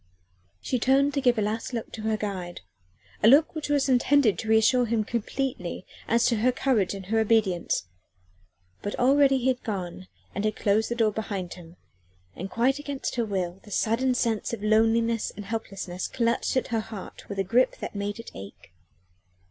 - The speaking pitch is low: No, high, 225 Hz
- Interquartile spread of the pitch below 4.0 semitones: Yes, average, 3.6 semitones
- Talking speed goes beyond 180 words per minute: Yes, average, 190 wpm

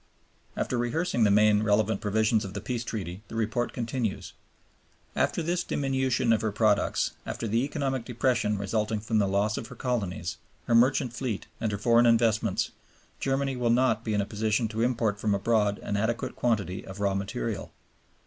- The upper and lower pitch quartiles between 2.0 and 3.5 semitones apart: Yes, average, 2.8 semitones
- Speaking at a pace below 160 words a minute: No, average, 175 wpm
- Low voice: Yes, low, 110 Hz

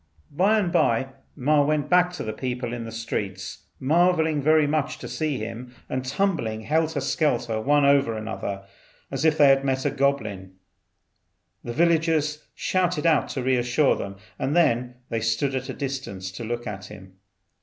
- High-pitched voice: No, low, 135 Hz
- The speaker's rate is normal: Yes, average, 170 wpm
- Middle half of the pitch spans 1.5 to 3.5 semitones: No, average, 5.1 semitones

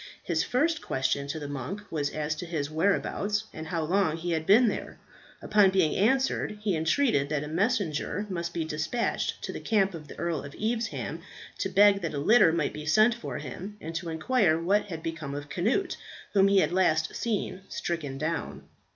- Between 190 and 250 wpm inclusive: Yes, average, 195 wpm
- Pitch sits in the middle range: Yes, medium, 170 Hz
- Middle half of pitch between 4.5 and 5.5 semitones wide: Yes, average, 4.9 semitones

